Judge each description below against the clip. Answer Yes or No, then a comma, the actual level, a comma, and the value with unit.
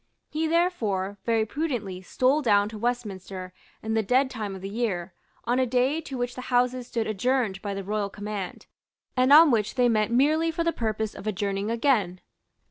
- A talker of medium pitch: No, high, 225 Hz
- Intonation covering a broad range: No, average, 4.2 semitones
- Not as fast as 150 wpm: No, average, 190 wpm